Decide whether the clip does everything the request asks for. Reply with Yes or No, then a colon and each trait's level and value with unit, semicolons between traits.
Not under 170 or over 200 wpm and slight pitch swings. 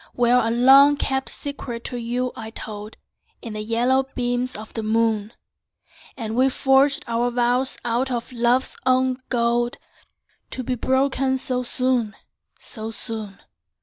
No: average, 145 wpm; narrow, 2.2 semitones